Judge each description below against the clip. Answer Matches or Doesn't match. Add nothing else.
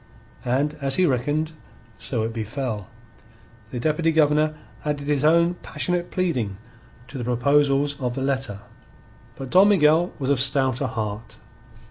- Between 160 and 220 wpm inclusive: Doesn't match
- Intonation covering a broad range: Doesn't match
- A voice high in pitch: Doesn't match